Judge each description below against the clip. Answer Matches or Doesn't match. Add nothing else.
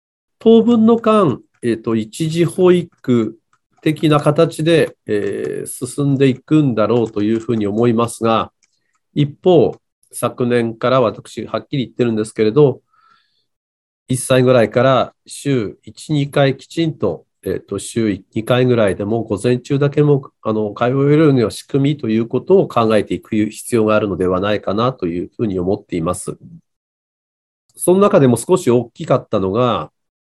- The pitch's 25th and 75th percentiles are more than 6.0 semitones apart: Doesn't match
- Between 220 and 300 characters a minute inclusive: Matches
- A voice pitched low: Matches